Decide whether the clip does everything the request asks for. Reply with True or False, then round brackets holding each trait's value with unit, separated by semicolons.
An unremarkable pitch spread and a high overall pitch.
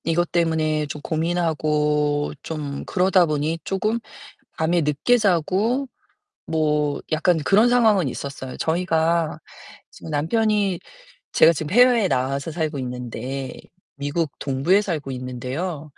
False (3.8 semitones; 160 Hz)